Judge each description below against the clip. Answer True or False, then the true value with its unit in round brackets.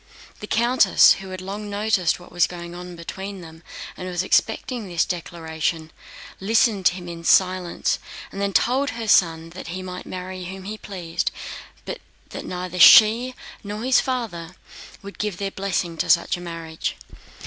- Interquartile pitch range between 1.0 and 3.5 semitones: True (3.1 semitones)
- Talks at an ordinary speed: True (170 wpm)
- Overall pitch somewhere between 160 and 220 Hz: True (185 Hz)